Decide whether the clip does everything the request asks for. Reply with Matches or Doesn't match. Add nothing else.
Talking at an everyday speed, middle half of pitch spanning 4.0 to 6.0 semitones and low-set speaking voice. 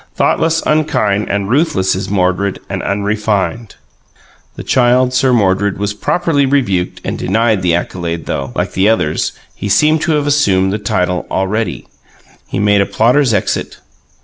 Matches